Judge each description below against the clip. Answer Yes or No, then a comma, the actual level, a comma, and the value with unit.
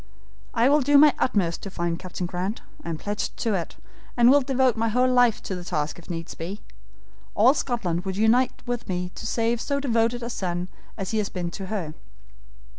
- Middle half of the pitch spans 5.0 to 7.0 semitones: Yes, wide, 5.4 semitones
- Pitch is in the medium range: No, high, 215 Hz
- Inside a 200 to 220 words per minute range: Yes, fast, 205 wpm